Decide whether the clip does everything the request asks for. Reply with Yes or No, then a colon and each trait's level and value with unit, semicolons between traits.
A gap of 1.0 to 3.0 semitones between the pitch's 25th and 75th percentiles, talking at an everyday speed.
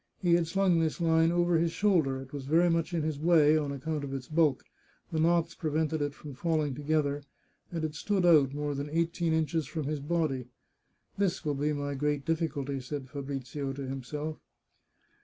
Yes: average, 2.7 semitones; average, 195 wpm